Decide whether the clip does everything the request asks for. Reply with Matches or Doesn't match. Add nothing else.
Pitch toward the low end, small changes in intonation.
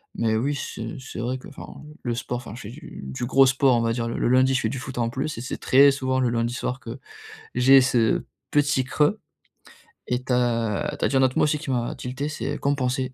Matches